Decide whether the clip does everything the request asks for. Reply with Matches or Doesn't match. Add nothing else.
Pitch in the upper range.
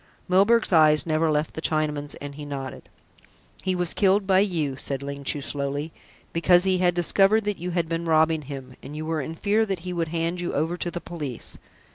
Doesn't match